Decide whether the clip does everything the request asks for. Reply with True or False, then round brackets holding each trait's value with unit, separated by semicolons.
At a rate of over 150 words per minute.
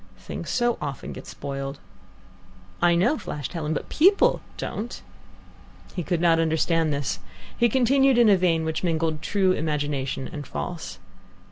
False (145 wpm)